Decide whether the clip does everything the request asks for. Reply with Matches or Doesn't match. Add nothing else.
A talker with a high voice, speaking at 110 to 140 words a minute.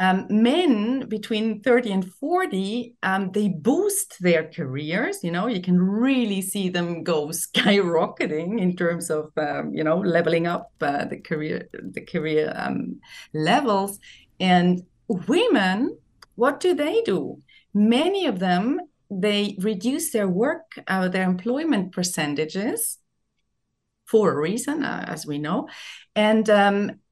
Matches